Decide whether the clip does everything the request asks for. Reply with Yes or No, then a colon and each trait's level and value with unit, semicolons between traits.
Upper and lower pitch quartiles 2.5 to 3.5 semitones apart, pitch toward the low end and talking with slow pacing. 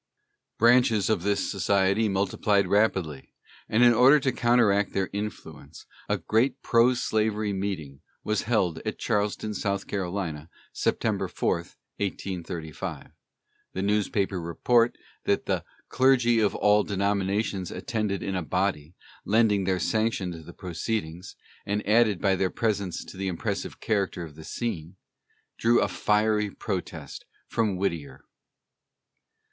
Yes: average, 3.0 semitones; low, 100 Hz; slow, 130 wpm